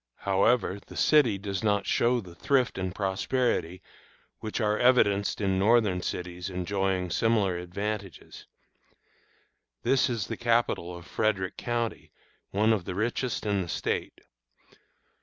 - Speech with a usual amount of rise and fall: Yes, average, 3.7 semitones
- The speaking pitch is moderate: No, low, 100 Hz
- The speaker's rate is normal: No, slow, 130 wpm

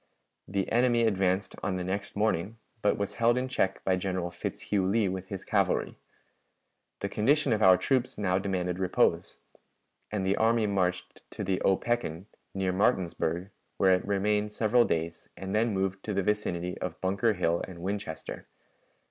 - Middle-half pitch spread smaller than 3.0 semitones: Yes, narrow, 2.5 semitones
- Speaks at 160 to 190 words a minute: Yes, average, 165 wpm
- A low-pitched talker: Yes, very low, 95 Hz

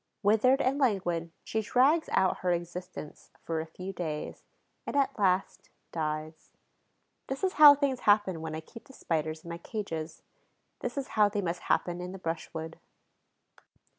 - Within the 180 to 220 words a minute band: No, average, 165 wpm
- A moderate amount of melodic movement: No, wide, 6.7 semitones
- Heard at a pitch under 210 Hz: Yes, medium, 185 Hz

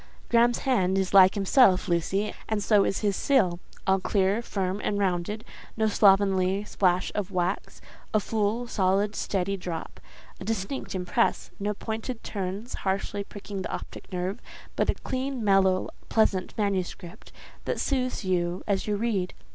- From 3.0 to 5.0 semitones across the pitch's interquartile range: No, narrow, 2.6 semitones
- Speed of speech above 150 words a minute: No, average, 140 wpm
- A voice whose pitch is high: Yes, high, 200 Hz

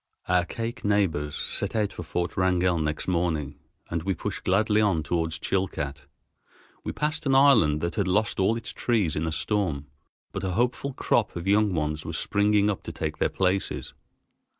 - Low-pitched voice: Yes, very low, 95 Hz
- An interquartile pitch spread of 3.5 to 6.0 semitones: Yes, average, 4.5 semitones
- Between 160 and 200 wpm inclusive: Yes, average, 180 wpm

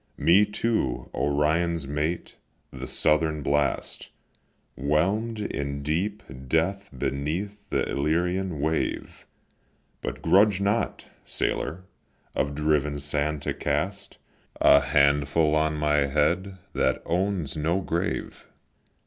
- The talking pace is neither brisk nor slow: No, slow, 105 wpm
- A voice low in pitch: Yes, very low, 80 Hz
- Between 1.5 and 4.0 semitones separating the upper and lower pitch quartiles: No, average, 4.5 semitones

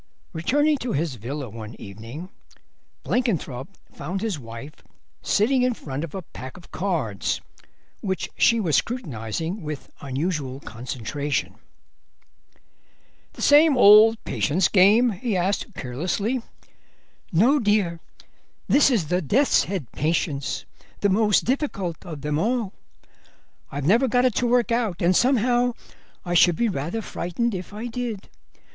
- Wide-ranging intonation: Yes, wide, 8.0 semitones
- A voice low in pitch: No, medium, 185 Hz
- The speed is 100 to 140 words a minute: Yes, slow, 135 wpm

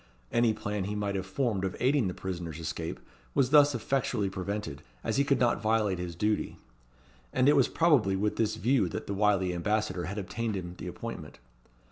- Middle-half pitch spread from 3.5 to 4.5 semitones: Yes, average, 4.2 semitones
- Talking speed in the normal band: Yes, average, 190 wpm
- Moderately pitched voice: No, low, 105 Hz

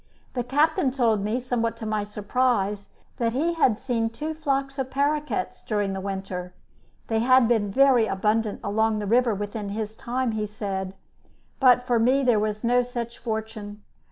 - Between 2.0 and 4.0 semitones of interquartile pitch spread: Yes, average, 3.4 semitones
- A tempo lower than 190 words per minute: Yes, average, 170 wpm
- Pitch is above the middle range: Yes, high, 225 Hz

